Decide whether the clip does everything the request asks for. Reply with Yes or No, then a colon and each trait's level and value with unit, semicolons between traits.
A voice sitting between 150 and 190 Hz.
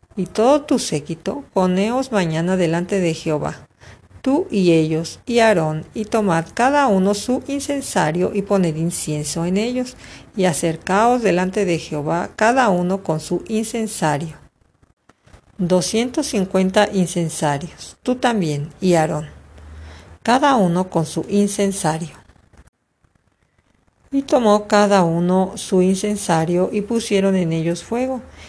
Yes: medium, 185 Hz